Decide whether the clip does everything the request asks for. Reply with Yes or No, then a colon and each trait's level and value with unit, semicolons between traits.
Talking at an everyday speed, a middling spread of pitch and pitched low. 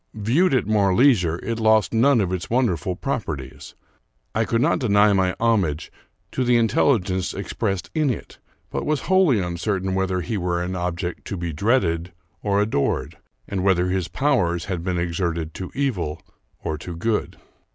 Yes: average, 170 wpm; average, 4.7 semitones; very low, 95 Hz